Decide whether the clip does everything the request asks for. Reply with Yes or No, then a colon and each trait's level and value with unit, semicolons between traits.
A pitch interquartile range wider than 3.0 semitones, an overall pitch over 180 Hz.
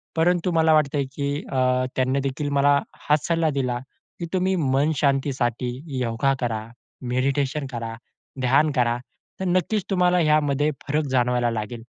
No: average, 3.4 semitones; medium, 140 Hz